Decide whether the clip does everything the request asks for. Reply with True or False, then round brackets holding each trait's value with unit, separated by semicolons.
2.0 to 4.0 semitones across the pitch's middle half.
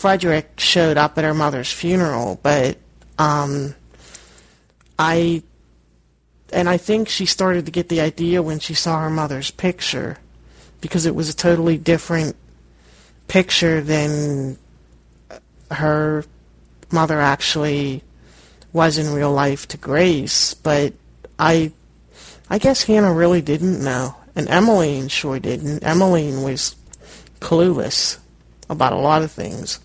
False (4.9 semitones)